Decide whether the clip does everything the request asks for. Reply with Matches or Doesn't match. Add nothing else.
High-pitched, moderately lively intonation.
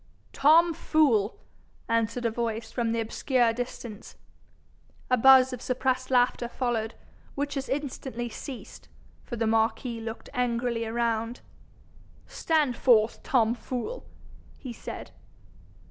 Doesn't match